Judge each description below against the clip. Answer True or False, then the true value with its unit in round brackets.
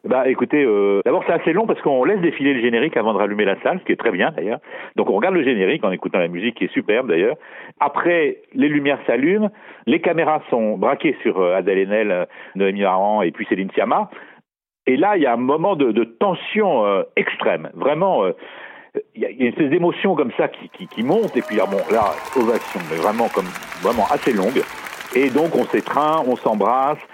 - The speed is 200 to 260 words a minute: True (215 wpm)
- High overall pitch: False (140 Hz)